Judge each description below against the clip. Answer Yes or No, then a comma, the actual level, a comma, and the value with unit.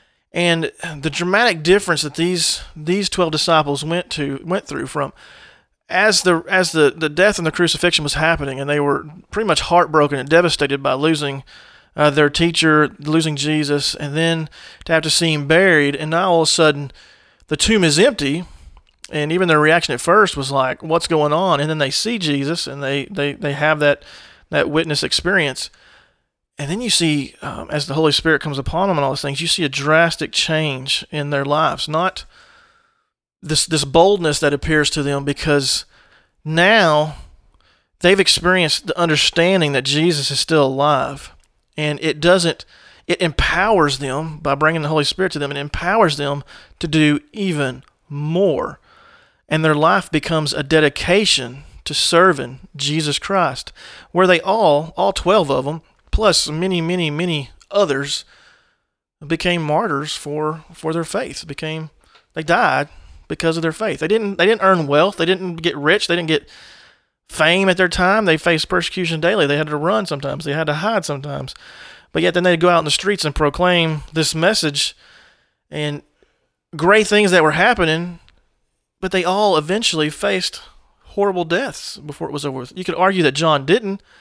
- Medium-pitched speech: Yes, medium, 160 Hz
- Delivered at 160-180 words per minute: Yes, average, 175 wpm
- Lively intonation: No, average, 3.3 semitones